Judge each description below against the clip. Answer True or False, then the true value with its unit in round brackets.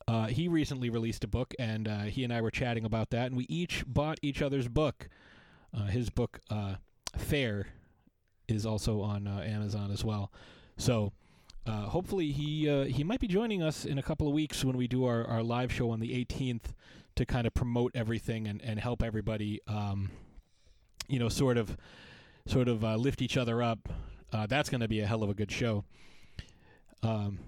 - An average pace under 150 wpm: False (200 wpm)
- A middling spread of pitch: True (3.5 semitones)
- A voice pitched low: True (115 Hz)